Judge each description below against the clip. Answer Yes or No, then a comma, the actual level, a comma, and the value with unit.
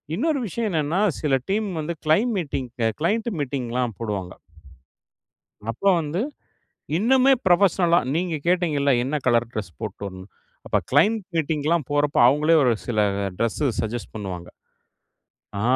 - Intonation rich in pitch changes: Yes, wide, 7.0 semitones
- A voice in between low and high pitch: Yes, medium, 150 Hz